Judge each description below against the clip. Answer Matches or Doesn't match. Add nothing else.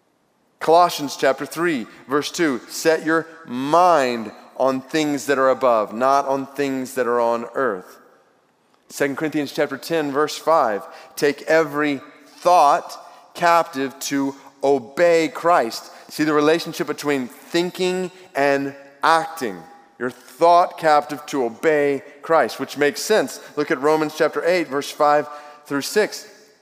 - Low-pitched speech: Doesn't match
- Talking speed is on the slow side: Matches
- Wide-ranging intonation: Doesn't match